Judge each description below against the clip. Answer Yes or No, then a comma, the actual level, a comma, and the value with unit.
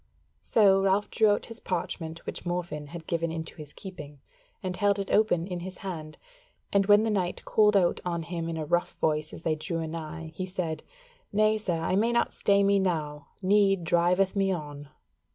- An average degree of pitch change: Yes, average, 3.5 semitones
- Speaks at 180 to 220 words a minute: Yes, average, 195 wpm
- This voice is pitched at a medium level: Yes, medium, 180 Hz